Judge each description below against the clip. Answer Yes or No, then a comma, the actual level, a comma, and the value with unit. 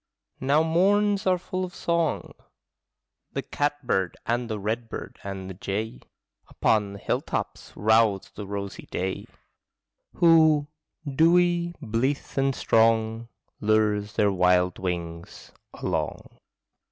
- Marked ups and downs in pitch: Yes, wide, 7.9 semitones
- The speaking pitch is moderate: No, low, 115 Hz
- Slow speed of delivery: Yes, slow, 110 wpm